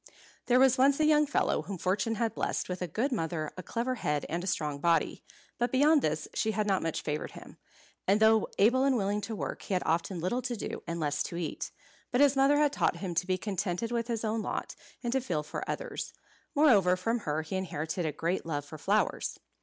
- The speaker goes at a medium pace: No, fast, 230 wpm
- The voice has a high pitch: Yes, high, 200 Hz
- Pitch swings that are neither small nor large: No, wide, 6.3 semitones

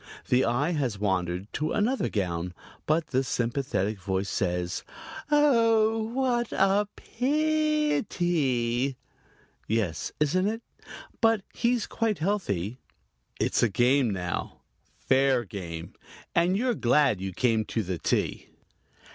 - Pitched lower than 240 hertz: Yes, low, 135 Hz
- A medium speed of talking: No, slow, 120 wpm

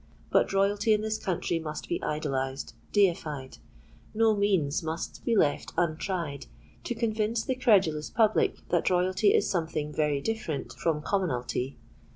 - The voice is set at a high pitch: No, medium, 175 Hz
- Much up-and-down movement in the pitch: Yes, wide, 5.7 semitones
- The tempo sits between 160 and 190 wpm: No, slow, 135 wpm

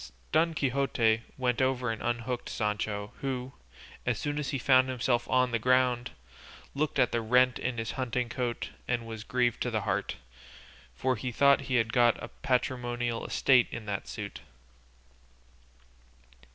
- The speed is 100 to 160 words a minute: Yes, average, 150 wpm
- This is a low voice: Yes, low, 125 Hz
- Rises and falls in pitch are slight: Yes, narrow, 1.8 semitones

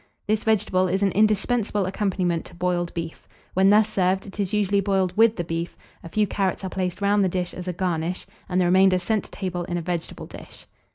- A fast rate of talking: Yes, fast, 220 wpm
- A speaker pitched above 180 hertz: Yes, high, 190 Hz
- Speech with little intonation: Yes, narrow, 2.3 semitones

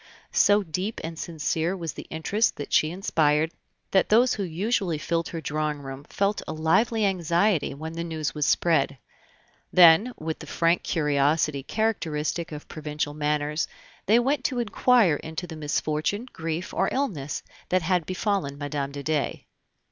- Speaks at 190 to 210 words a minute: No, average, 155 wpm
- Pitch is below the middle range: No, medium, 160 Hz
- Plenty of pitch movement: No, average, 4.3 semitones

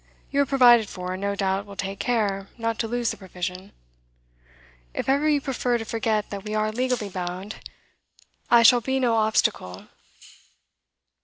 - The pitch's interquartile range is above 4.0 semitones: No, average, 3.6 semitones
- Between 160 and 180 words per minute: Yes, average, 165 wpm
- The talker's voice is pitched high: Yes, high, 215 Hz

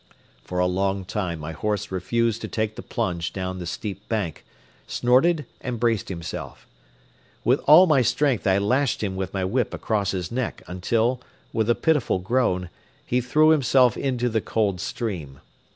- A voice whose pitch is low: Yes, low, 110 Hz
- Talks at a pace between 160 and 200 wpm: Yes, average, 170 wpm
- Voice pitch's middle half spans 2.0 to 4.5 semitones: No, average, 4.9 semitones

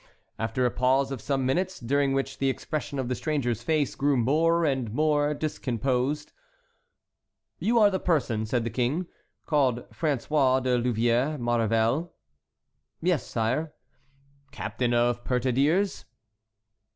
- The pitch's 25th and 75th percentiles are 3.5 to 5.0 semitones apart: Yes, average, 3.9 semitones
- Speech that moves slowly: Yes, slow, 125 wpm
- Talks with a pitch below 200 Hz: Yes, low, 135 Hz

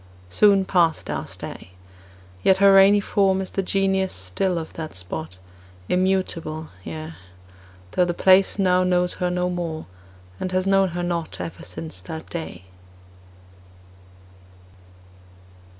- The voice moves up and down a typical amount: Yes, average, 3.0 semitones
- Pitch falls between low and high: Yes, medium, 180 Hz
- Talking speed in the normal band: No, slow, 130 wpm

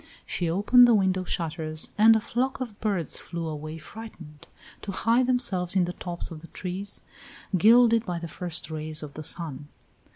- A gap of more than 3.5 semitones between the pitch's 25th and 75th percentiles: Yes, wide, 5.5 semitones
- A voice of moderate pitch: Yes, medium, 180 Hz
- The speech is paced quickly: No, average, 175 wpm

